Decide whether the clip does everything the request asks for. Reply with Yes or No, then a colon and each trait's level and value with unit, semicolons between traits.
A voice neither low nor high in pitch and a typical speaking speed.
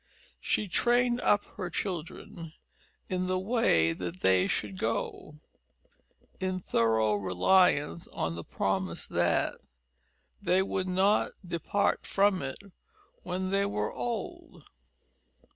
No: medium, 180 Hz; slow, 110 wpm